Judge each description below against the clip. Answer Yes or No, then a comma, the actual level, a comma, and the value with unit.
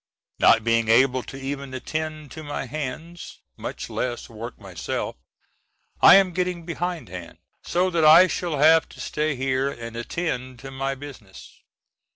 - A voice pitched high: No, medium, 140 Hz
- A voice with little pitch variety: No, average, 4.6 semitones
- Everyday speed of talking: Yes, average, 150 wpm